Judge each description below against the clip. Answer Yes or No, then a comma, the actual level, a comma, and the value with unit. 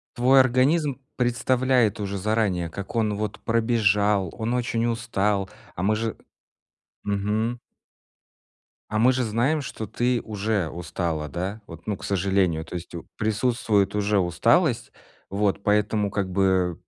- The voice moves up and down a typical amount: Yes, average, 3.3 semitones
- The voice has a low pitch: Yes, low, 105 Hz